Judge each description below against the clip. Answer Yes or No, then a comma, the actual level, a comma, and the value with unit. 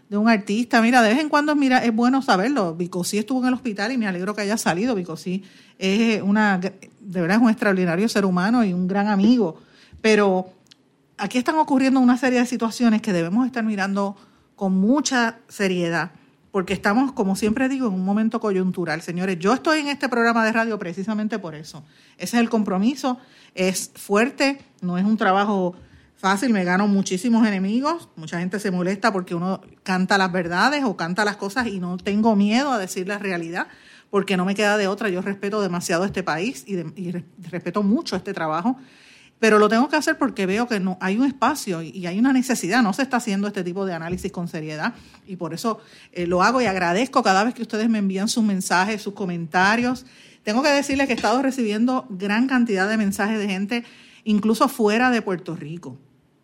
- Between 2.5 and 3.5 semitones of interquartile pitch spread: No, average, 4.2 semitones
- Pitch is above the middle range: Yes, high, 205 Hz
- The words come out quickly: Yes, fast, 205 wpm